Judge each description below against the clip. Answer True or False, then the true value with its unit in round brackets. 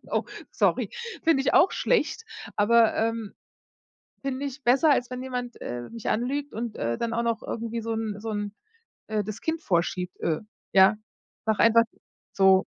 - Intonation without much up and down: False (3.6 semitones)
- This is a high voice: True (230 Hz)